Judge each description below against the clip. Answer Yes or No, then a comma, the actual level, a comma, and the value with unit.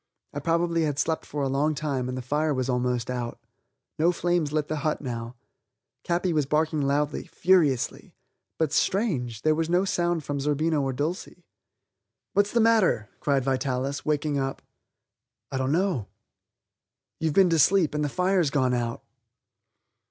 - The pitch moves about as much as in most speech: Yes, average, 4.0 semitones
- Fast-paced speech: No, average, 160 wpm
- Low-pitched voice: No, medium, 150 Hz